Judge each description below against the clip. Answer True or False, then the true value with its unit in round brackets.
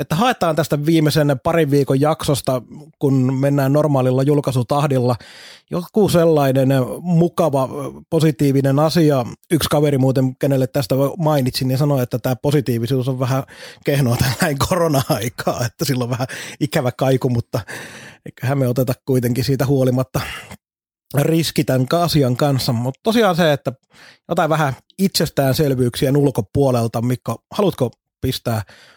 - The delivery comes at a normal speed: True (125 wpm)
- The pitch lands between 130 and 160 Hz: True (140 Hz)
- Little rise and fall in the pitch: False (3.0 semitones)